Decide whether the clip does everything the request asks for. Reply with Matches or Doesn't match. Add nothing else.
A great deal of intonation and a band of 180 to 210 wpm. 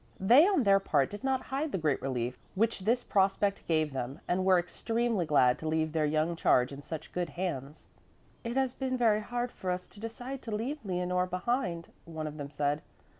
Matches